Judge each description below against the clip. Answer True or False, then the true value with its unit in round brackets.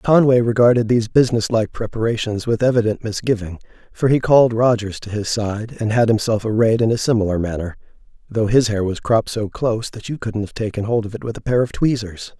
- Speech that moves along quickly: True (215 wpm)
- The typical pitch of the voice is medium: False (110 Hz)